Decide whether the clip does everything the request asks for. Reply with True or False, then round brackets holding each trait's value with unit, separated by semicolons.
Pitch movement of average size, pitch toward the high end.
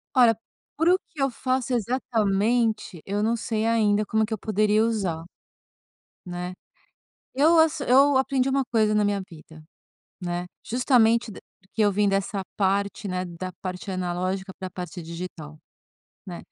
True (4.4 semitones; 210 Hz)